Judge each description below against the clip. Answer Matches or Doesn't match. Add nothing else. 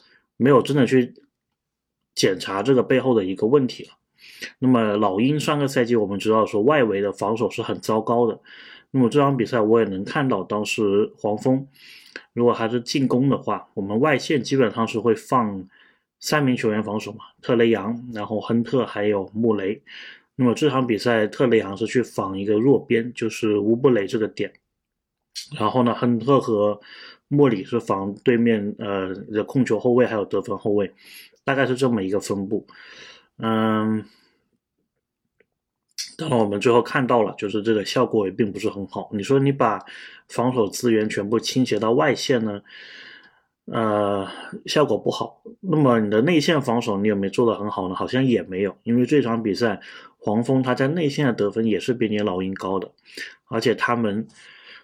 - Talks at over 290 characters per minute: Doesn't match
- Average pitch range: Matches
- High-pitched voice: Doesn't match